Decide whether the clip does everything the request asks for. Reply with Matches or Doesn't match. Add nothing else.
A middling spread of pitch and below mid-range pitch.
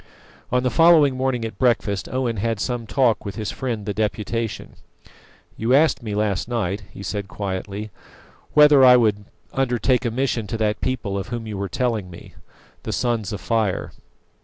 Matches